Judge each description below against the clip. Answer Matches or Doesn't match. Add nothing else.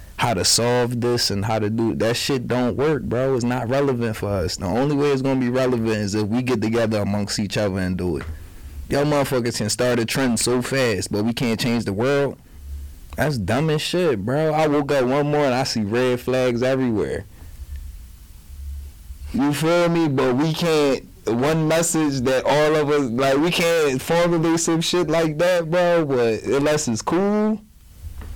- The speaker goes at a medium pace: Matches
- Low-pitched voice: Matches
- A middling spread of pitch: Doesn't match